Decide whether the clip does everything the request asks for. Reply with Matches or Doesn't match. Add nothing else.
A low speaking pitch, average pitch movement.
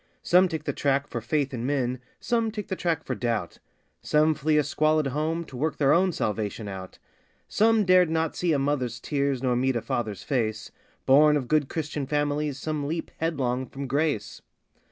Doesn't match